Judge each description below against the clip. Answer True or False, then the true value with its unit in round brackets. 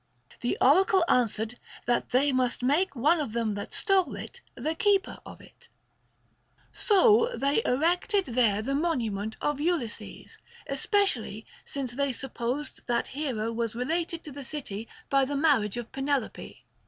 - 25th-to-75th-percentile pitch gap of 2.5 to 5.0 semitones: False (5.6 semitones)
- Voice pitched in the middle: False (275 Hz)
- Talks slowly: False (145 wpm)